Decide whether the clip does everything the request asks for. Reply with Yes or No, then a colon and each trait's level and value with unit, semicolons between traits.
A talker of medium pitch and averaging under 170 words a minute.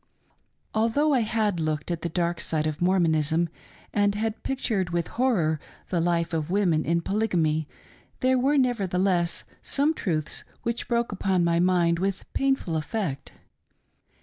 Yes: medium, 180 Hz; average, 145 wpm